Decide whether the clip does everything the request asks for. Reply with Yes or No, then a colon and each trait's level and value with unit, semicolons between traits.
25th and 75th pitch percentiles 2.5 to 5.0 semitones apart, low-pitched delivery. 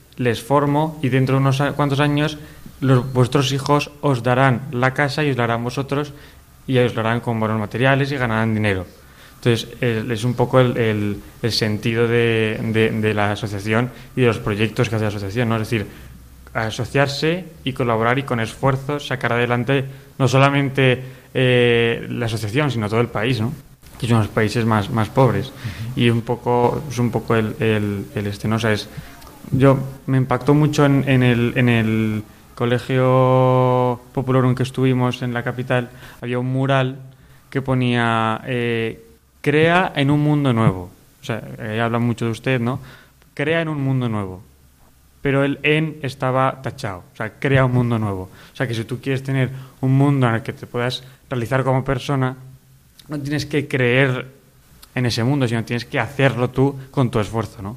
Yes: average, 3.0 semitones; low, 125 Hz